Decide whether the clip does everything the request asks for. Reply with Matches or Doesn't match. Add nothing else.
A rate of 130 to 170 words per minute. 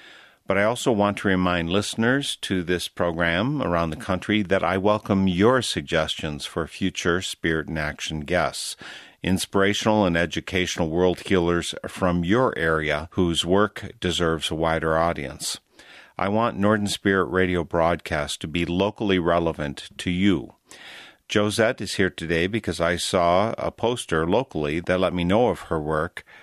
Matches